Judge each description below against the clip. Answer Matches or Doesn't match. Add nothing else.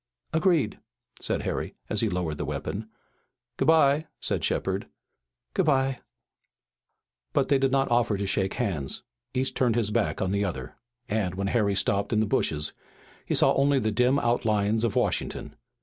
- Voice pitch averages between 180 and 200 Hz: Doesn't match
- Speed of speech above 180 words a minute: Doesn't match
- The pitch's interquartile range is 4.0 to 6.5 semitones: Matches